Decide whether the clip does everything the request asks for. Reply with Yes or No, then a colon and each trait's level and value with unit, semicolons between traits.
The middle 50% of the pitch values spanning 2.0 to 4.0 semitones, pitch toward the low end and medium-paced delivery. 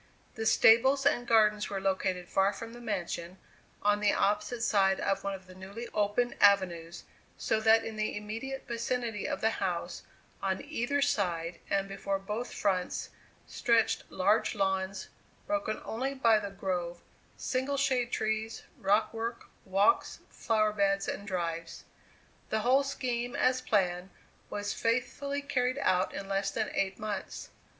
No: average, 3.5 semitones; high, 210 Hz; average, 150 wpm